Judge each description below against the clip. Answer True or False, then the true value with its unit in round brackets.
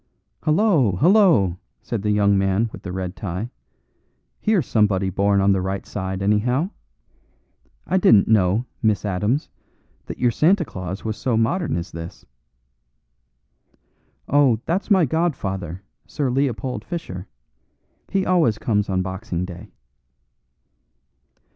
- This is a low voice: True (105 Hz)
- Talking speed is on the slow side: True (125 wpm)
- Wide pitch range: True (7.1 semitones)